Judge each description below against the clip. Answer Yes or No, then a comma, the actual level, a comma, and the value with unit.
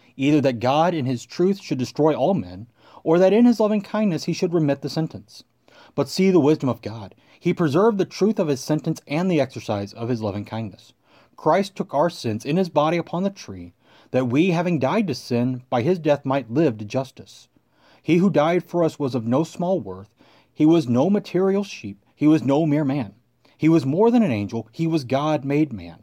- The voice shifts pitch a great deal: Yes, wide, 6.0 semitones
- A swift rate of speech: Yes, fast, 220 wpm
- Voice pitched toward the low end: No, medium, 150 Hz